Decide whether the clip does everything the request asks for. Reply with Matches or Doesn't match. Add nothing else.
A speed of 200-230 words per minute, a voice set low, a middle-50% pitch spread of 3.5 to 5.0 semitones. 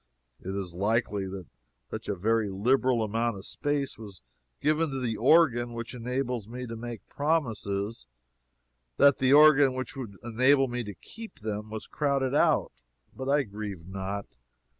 Doesn't match